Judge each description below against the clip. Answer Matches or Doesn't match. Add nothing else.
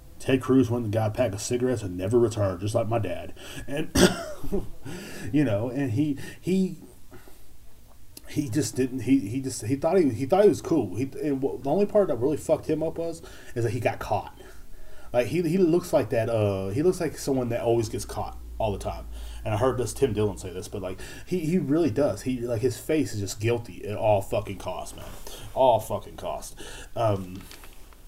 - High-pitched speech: Doesn't match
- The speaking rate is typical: Doesn't match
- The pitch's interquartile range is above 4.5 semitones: Matches